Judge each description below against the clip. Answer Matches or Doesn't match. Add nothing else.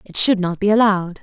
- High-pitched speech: Matches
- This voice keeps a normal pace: Doesn't match